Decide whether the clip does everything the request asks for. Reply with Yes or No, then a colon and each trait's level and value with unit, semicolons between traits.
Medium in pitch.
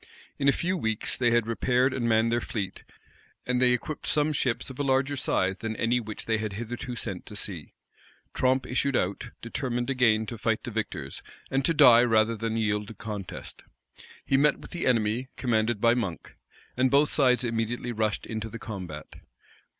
No: low, 120 Hz